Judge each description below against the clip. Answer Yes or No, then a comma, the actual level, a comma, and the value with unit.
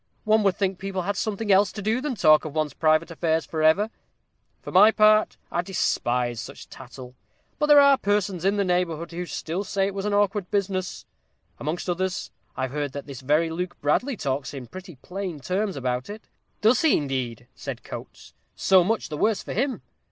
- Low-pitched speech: No, medium, 180 Hz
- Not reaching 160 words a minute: No, average, 195 wpm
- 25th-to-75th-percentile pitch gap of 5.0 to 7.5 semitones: Yes, average, 5.3 semitones